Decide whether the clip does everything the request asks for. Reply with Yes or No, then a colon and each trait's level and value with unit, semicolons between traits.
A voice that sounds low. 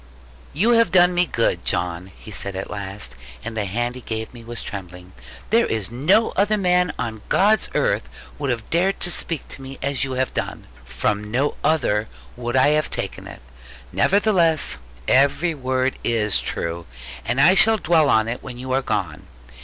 Yes: low, 130 Hz